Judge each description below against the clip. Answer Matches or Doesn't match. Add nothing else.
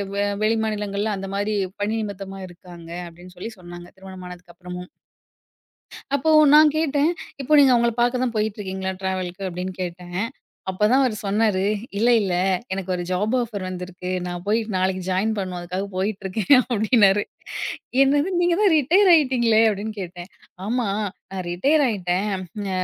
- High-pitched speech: Matches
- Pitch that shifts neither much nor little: Matches